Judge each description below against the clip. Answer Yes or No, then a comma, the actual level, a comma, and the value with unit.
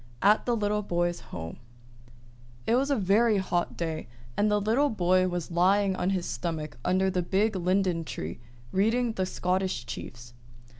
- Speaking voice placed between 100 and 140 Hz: No, medium, 185 Hz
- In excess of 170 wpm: No, average, 160 wpm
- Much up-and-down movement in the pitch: No, average, 3.2 semitones